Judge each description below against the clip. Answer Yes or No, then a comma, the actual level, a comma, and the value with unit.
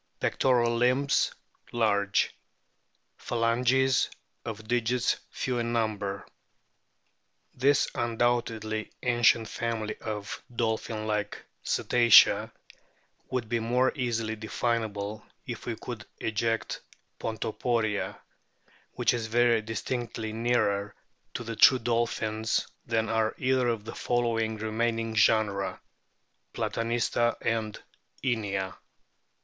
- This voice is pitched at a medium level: No, low, 115 Hz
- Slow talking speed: Yes, slow, 95 wpm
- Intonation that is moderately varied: No, narrow, 1.7 semitones